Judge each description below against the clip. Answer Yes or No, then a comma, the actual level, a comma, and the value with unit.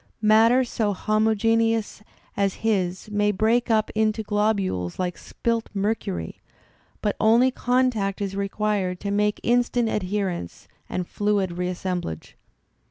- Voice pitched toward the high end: Yes, high, 210 Hz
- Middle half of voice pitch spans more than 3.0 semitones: No, average, 2.7 semitones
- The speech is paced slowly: Yes, slow, 120 wpm